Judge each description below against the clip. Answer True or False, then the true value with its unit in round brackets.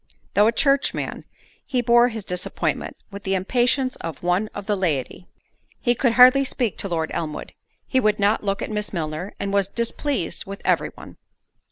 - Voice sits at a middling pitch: False (205 Hz)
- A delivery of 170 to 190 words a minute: True (180 wpm)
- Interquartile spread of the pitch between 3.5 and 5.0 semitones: True (4.6 semitones)